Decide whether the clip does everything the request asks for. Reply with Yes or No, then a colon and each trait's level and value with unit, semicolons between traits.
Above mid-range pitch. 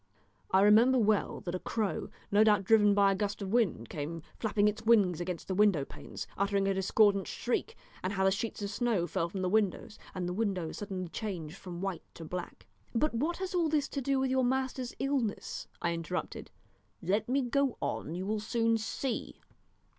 Yes: high, 205 Hz